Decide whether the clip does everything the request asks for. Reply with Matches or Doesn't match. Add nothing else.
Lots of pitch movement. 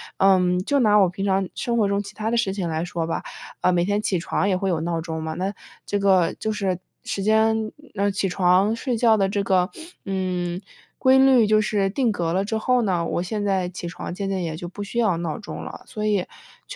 Doesn't match